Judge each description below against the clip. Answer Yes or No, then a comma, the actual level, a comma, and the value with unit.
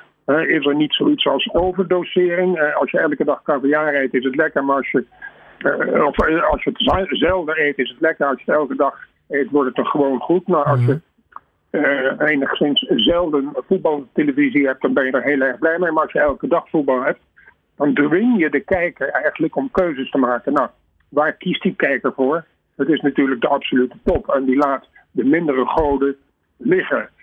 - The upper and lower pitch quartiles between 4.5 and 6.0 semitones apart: Yes, average, 4.8 semitones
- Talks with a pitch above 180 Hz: No, medium, 150 Hz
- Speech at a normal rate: No, fast, 210 wpm